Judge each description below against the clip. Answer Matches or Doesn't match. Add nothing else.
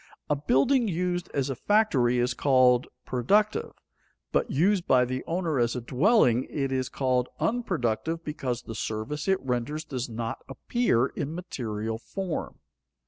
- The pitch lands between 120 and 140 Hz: Matches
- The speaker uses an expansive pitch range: Matches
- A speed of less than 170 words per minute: Matches